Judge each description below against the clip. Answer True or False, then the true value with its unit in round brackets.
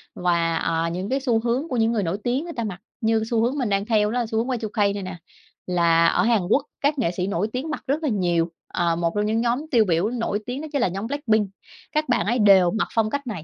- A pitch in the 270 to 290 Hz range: False (220 Hz)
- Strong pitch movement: False (5.0 semitones)